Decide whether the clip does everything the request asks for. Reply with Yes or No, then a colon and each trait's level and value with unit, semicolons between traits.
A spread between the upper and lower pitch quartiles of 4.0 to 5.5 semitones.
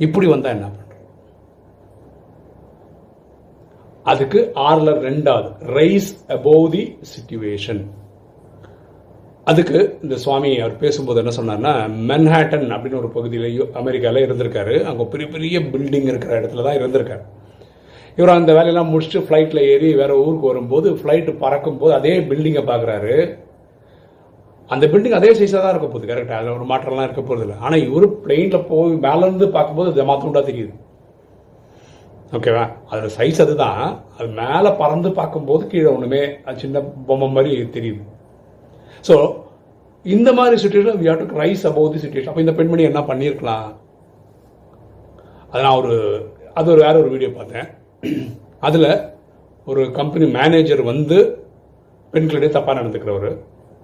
Yes: average, 5.2 semitones